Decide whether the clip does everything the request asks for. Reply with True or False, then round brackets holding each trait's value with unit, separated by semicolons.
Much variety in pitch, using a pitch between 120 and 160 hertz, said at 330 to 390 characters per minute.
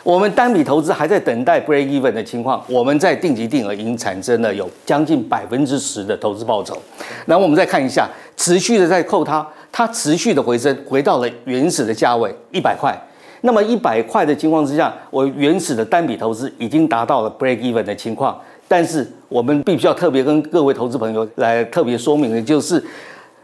False (5.0 semitones; 140 Hz; 345 characters per minute)